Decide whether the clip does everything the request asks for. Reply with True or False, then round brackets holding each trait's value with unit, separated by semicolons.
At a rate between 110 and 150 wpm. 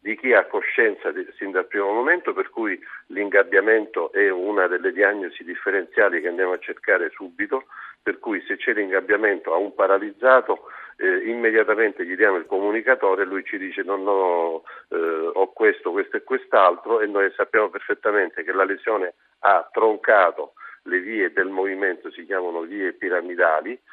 False (165 wpm)